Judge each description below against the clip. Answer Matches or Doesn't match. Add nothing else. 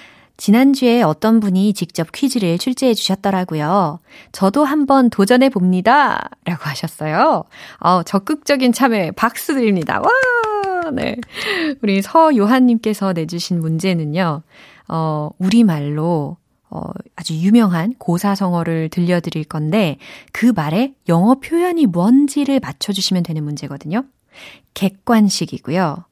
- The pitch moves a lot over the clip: Matches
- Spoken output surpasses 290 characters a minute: Doesn't match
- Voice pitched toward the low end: Doesn't match